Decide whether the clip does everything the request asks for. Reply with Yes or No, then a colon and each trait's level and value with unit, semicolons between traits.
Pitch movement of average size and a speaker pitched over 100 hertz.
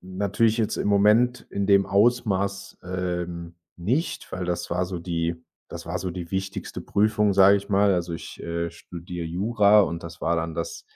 No: average, 3.1 semitones; very low, 95 Hz